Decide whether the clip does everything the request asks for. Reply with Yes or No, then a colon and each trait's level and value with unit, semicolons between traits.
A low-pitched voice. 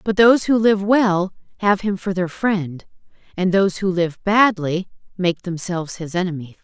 No: high, 190 Hz